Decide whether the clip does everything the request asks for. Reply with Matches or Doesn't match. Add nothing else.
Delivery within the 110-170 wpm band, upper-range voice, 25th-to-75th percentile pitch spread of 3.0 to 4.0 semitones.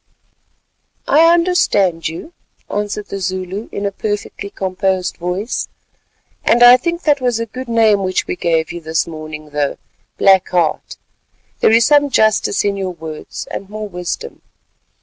Doesn't match